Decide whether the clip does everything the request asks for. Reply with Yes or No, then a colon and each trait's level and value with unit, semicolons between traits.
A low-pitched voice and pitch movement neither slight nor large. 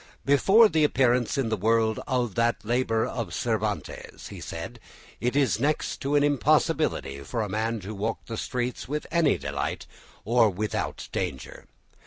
Yes: low, 115 Hz; average, 3.9 semitones